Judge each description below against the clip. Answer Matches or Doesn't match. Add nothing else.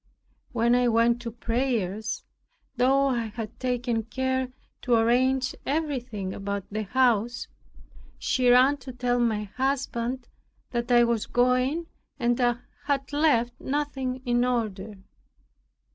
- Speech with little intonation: Matches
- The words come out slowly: Matches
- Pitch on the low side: Doesn't match